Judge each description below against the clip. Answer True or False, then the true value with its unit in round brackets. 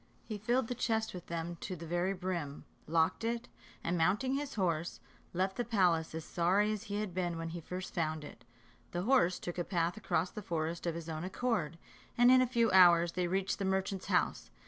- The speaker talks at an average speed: False (215 wpm)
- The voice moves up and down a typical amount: True (3.9 semitones)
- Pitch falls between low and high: True (180 Hz)